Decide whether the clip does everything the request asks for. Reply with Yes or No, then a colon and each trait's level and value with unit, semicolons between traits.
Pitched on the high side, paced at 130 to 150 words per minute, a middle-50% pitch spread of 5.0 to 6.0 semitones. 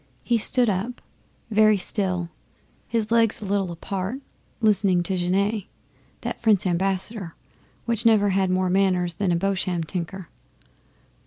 No: high, 195 Hz; slow, 135 wpm; average, 2.8 semitones